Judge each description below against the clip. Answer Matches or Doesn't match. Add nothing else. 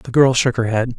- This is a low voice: Matches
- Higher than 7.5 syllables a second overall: Doesn't match